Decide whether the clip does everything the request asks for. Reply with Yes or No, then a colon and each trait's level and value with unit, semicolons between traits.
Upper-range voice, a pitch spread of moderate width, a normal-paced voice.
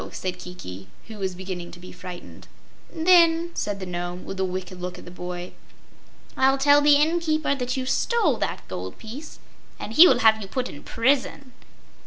No: high, 220 Hz; wide, 8.1 semitones; average, 190 wpm